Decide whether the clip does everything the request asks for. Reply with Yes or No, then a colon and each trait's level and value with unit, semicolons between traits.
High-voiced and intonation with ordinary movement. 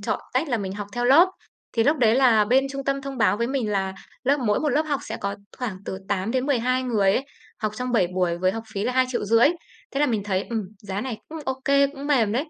Yes: high, 240 Hz; average, 4.7 semitones